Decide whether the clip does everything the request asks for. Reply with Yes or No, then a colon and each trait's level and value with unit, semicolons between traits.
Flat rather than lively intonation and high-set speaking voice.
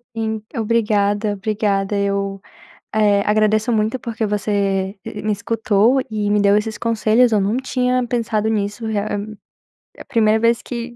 Yes: narrow, 2.0 semitones; high, 215 Hz